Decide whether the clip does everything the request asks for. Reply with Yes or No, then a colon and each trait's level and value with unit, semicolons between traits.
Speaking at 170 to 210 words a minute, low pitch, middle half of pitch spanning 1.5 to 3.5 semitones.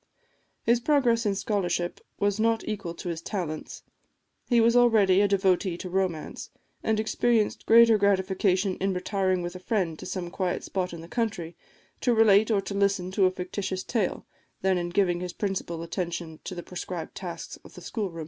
No: average, 180 wpm; high, 190 Hz; average, 3.1 semitones